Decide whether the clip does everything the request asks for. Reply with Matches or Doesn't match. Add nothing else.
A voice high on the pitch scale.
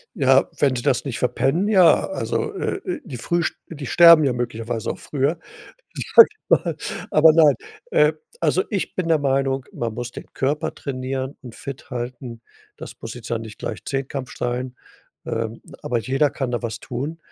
Doesn't match